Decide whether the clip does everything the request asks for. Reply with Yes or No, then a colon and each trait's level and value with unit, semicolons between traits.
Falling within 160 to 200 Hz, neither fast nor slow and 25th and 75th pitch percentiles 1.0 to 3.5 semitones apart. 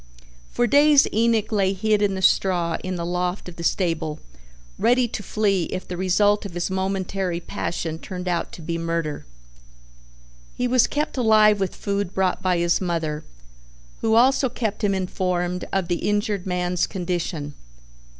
Yes: high, 190 Hz; average, 160 wpm; average, 3.1 semitones